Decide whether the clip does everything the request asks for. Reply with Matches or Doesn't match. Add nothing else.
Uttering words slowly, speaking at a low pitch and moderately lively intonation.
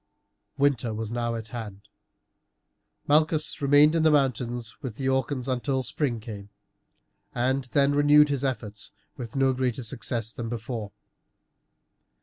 Matches